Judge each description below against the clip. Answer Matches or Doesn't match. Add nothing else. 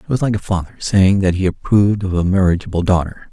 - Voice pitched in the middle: Doesn't match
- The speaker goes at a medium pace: Doesn't match